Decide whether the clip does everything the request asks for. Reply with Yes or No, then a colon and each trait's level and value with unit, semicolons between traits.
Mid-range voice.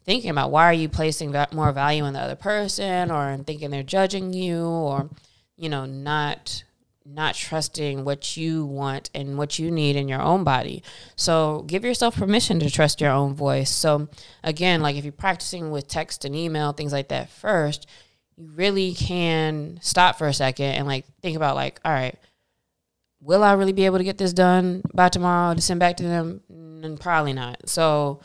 Yes: medium, 155 Hz